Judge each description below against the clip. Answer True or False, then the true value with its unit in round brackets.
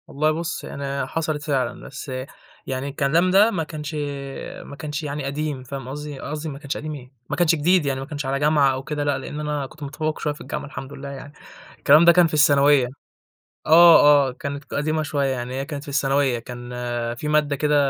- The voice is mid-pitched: True (145 Hz)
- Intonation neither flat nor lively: False (1.9 semitones)